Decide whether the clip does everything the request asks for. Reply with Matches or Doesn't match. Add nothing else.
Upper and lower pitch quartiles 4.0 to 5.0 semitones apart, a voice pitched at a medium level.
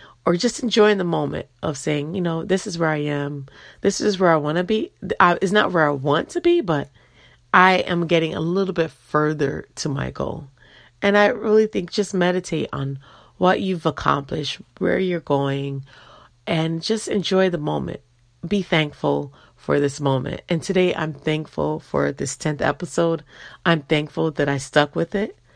Matches